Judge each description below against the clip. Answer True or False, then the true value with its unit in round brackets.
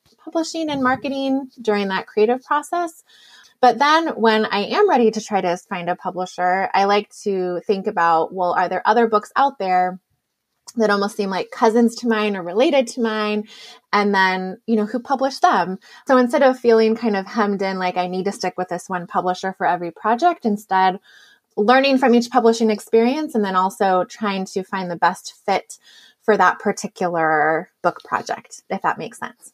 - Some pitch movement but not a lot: True (4.7 semitones)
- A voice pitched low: False (210 Hz)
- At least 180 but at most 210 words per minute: True (190 wpm)